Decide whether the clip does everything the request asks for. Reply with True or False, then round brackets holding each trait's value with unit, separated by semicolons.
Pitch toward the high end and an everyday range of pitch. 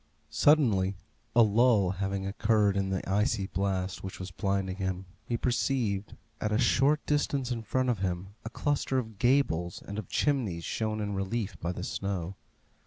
False (100 Hz; 3.8 semitones)